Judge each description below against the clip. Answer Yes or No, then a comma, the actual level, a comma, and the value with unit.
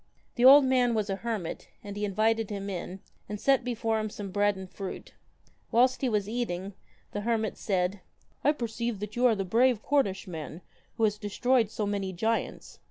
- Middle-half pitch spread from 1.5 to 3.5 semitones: Yes, average, 3.2 semitones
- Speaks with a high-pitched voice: Yes, high, 215 Hz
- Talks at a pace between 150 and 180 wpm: No, average, 190 wpm